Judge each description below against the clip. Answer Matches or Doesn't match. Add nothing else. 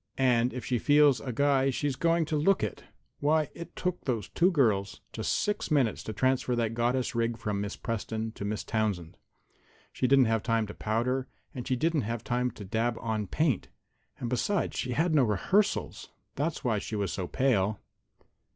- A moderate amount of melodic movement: Matches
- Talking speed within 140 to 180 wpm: Doesn't match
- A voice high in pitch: Doesn't match